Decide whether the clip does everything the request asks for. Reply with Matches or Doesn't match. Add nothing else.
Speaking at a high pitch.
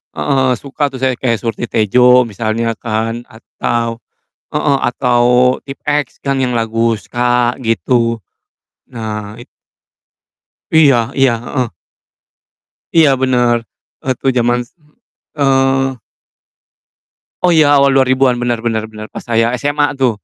Doesn't match